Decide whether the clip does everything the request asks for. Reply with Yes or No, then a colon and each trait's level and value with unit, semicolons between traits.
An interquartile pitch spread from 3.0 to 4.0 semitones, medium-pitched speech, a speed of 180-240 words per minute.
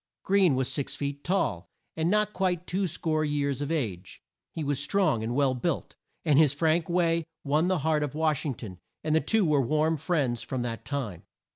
Yes: average, 3.7 semitones; medium, 150 Hz; average, 200 wpm